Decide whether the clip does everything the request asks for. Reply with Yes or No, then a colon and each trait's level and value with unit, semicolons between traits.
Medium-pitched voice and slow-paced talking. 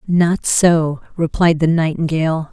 Yes: medium, 165 Hz; slow, 120 wpm